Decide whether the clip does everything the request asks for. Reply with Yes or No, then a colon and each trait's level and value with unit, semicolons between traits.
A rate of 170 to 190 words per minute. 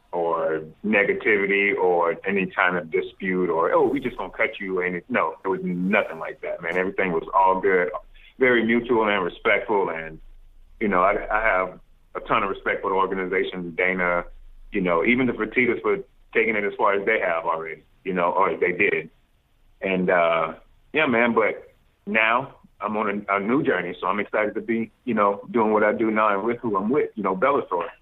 No: fast, 205 wpm